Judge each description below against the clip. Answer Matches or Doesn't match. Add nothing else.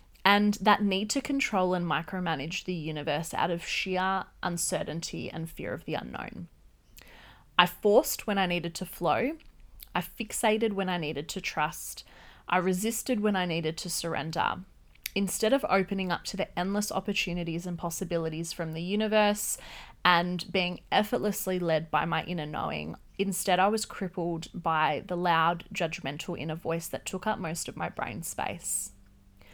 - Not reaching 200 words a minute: Matches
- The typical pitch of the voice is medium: Matches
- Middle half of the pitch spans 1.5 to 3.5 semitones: Matches